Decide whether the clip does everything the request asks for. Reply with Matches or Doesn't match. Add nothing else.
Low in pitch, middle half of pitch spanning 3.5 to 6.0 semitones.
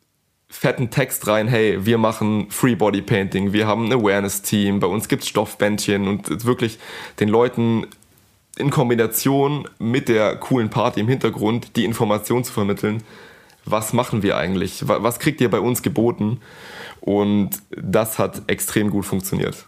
Doesn't match